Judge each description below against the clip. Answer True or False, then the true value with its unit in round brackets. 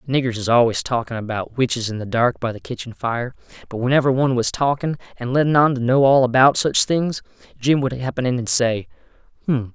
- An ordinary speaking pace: False (210 wpm)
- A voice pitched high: False (125 Hz)